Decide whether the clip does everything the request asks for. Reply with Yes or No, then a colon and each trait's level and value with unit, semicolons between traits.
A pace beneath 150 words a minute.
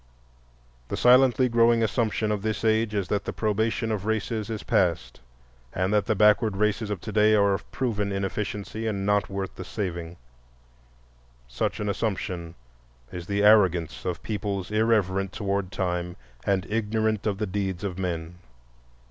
No: average, 155 wpm